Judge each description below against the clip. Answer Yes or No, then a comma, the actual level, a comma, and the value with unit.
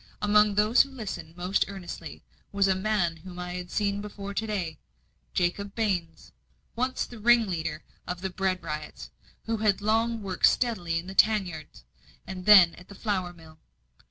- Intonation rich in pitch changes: No, average, 3.2 semitones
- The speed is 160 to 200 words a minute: Yes, average, 170 wpm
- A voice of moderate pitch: No, high, 195 Hz